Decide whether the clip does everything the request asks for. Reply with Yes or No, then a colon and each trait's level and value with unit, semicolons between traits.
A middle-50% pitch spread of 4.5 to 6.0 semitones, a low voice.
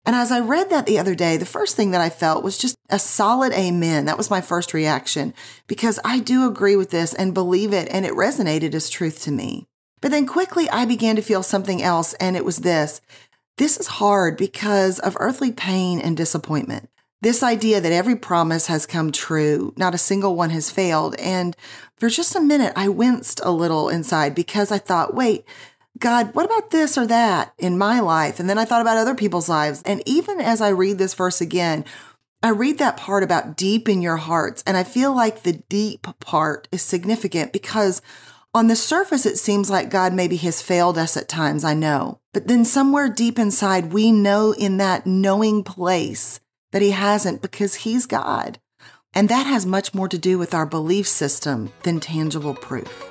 No: average, 5.0 semitones; high, 195 Hz